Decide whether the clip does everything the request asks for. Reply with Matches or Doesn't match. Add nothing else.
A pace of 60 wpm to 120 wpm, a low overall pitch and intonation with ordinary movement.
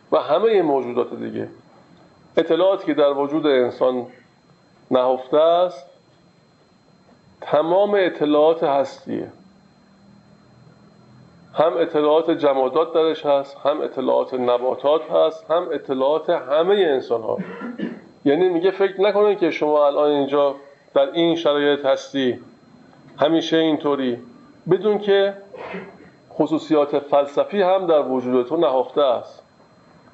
Doesn't match